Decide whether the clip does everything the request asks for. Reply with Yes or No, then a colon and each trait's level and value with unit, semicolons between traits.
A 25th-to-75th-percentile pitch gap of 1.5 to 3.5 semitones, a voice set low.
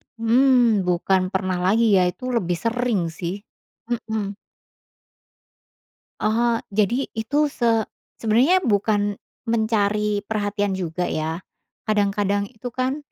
No: average, 2.7 semitones; high, 215 Hz